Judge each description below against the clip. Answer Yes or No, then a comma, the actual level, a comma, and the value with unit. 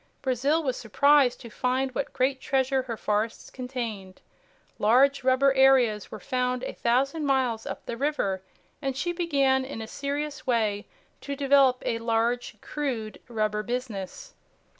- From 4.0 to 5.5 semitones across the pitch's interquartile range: No, average, 3.3 semitones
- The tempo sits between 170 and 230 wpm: No, average, 145 wpm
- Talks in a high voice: Yes, very high, 255 Hz